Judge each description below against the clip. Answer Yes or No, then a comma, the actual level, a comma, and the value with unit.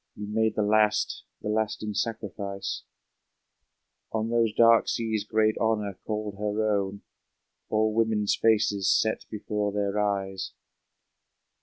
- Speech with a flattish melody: Yes, narrow, 1.3 semitones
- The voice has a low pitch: Yes, low, 105 Hz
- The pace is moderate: No, slow, 120 wpm